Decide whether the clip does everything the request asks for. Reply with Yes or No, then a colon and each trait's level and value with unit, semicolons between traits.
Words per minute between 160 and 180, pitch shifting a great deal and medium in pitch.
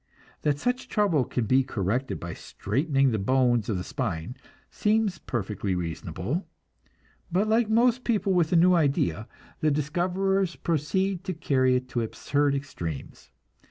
No: average, 145 wpm; wide, 7.9 semitones; medium, 145 Hz